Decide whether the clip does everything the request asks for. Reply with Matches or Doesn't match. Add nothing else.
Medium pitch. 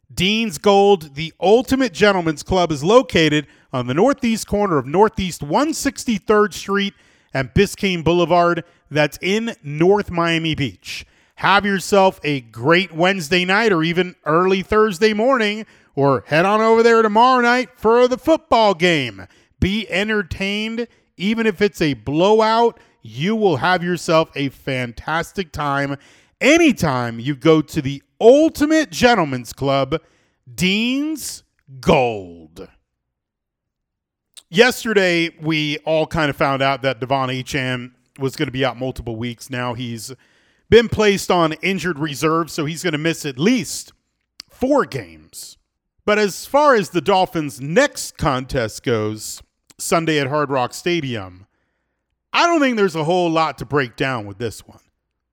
Matches